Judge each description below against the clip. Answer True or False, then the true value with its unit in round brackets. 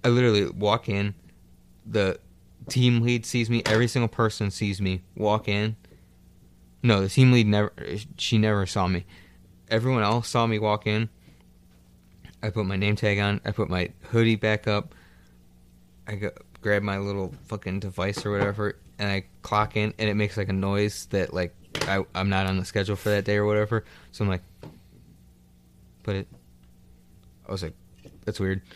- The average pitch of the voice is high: False (100 Hz)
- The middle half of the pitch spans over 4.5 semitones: False (2.9 semitones)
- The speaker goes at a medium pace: True (175 wpm)